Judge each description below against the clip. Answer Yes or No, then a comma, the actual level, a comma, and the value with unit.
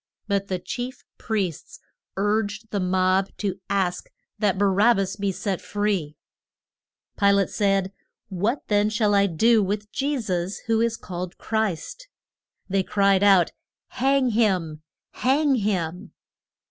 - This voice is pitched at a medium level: No, high, 200 Hz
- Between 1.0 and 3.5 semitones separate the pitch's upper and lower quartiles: Yes, average, 2.7 semitones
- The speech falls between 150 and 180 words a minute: No, slow, 135 wpm